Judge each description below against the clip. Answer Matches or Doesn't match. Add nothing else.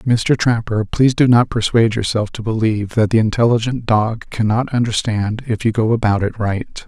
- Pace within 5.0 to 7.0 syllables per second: Matches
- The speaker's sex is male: Matches